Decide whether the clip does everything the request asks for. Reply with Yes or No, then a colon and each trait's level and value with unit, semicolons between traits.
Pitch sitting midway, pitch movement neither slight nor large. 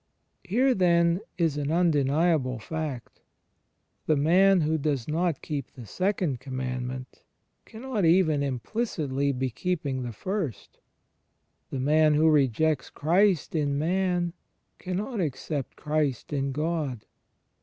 Yes: medium, 155 Hz; average, 4.5 semitones